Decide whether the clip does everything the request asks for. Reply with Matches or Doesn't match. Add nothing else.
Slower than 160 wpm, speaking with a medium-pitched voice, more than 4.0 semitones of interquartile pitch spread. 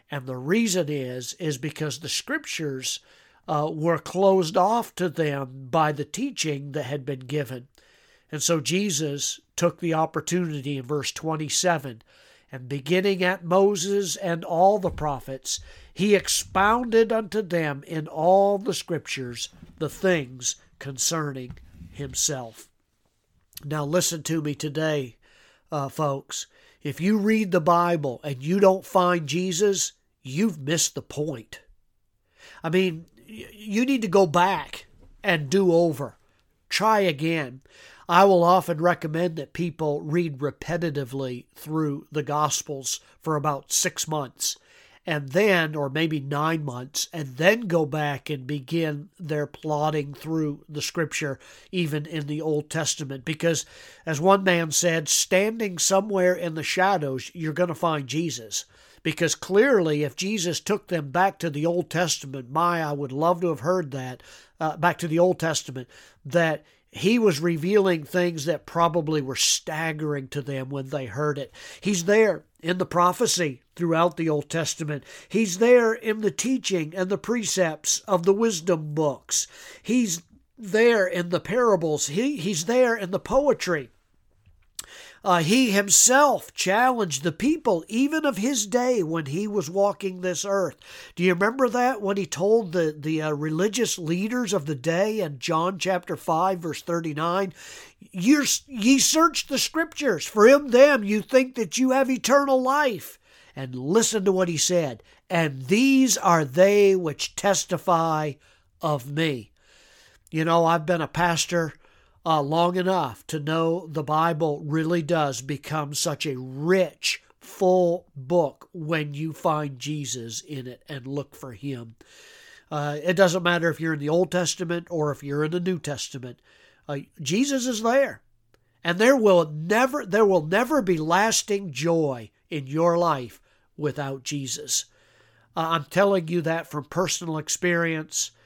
Matches